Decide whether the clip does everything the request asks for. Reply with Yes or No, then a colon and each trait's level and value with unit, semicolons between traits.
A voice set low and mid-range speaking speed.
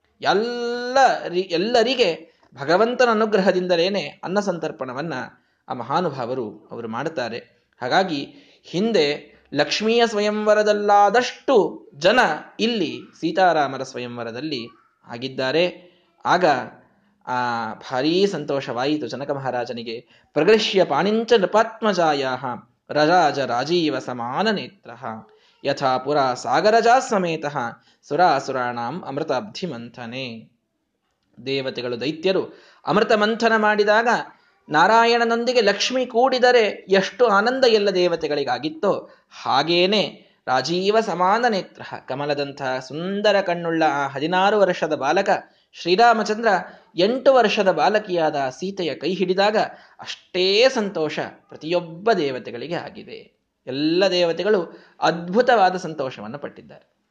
No: medium, 185 Hz; average, 80 wpm